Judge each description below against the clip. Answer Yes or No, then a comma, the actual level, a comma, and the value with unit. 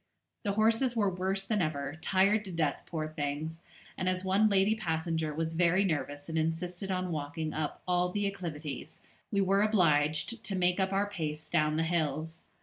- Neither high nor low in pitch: Yes, medium, 175 Hz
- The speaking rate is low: No, average, 180 wpm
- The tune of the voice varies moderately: Yes, average, 3.8 semitones